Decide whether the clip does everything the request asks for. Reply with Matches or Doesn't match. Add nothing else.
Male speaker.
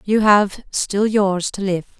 Doesn't match